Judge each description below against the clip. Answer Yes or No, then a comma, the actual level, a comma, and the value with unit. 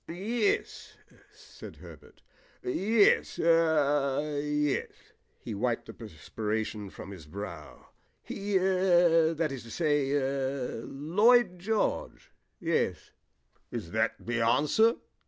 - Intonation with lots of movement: Yes, wide, 7.5 semitones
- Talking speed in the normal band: No, slow, 105 wpm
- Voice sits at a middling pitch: Yes, medium, 150 Hz